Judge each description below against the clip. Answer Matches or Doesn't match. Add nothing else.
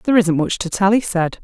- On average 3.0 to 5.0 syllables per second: Doesn't match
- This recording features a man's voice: Doesn't match